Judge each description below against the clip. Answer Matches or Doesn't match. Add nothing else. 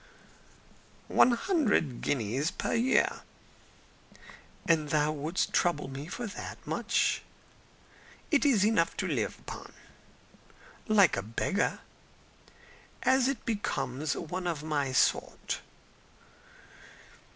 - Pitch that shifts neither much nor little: Doesn't match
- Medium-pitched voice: Matches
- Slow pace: Matches